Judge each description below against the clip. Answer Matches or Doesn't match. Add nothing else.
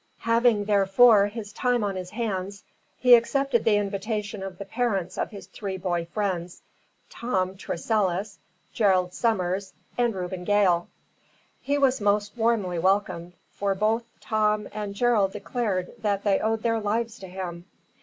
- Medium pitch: Doesn't match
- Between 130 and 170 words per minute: Matches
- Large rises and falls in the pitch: Doesn't match